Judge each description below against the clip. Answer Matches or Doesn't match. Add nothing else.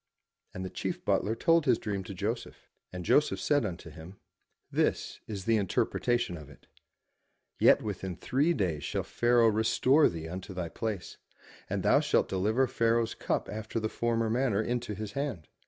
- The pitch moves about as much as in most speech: Matches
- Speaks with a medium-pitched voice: Doesn't match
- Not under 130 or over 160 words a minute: Doesn't match